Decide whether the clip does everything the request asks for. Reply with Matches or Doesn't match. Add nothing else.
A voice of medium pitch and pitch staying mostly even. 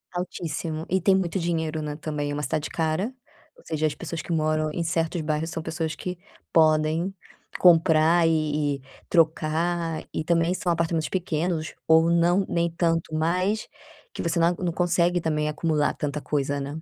Matches